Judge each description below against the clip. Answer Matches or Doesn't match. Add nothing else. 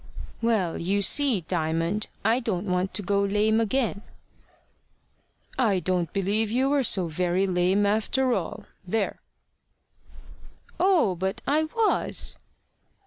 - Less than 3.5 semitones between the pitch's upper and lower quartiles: Doesn't match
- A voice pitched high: Matches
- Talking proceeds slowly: Matches